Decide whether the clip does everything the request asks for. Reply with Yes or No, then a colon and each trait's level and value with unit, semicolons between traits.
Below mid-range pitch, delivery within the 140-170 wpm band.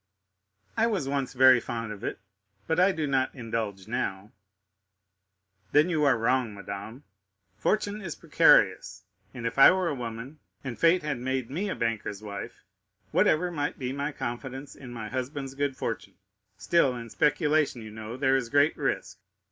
Yes: low, 130 Hz; average, 165 wpm